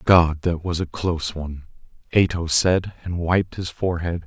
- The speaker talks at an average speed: Yes, average, 170 wpm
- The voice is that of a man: Yes, male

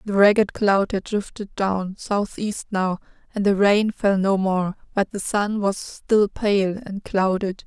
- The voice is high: Yes, high, 200 Hz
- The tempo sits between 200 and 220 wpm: No, average, 170 wpm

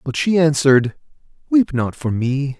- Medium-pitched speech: Yes, medium, 145 Hz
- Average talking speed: Yes, average, 160 wpm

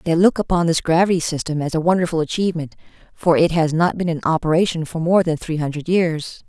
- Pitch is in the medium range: Yes, medium, 165 Hz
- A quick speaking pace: Yes, fast, 215 wpm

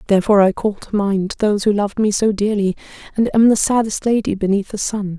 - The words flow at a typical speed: No, fast, 220 wpm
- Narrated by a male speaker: No, female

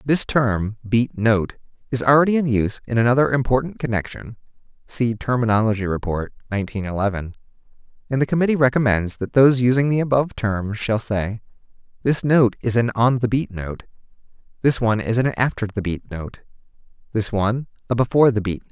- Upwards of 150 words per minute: Yes, average, 165 wpm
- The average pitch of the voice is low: Yes, low, 115 Hz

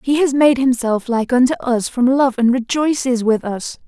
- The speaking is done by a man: No, female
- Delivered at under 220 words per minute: Yes, average, 200 wpm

